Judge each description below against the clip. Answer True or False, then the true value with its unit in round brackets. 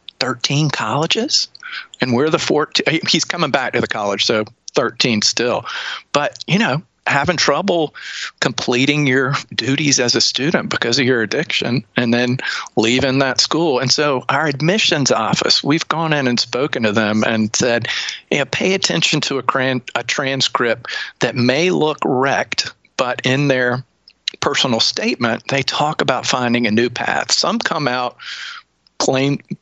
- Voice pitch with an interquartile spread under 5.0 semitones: True (4.0 semitones)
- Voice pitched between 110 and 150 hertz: True (135 Hz)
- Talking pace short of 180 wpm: True (155 wpm)